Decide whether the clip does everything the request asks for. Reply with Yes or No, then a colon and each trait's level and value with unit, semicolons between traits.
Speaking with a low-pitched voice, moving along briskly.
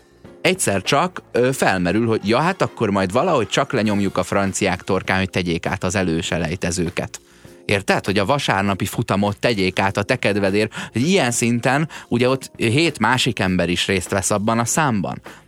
Yes: low, 100 Hz; fast, 170 wpm